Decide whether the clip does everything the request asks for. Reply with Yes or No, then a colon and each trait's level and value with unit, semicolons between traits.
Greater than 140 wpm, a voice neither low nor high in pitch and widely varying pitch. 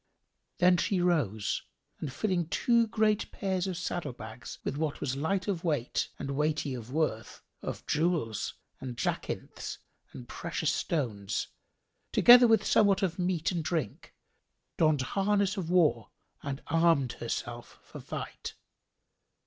No: slow, 135 wpm; medium, 160 Hz; wide, 5.9 semitones